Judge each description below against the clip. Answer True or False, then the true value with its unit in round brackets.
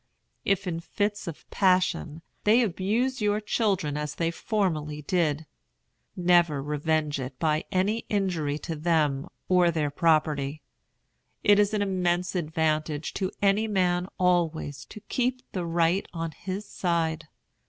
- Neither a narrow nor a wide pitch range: True (4.1 semitones)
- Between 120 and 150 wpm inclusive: True (135 wpm)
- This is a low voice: False (170 Hz)